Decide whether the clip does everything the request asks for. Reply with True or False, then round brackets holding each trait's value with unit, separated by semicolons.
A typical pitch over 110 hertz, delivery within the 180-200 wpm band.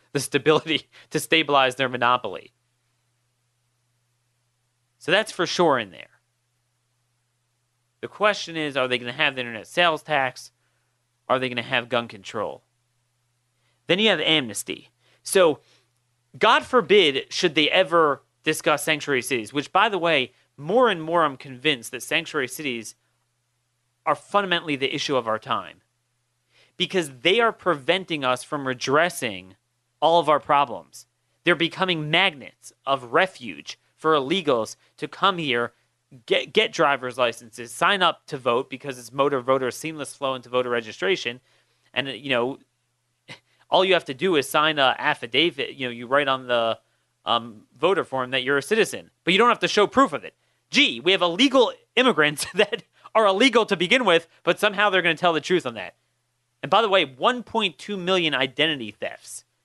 False (135 Hz; 165 wpm)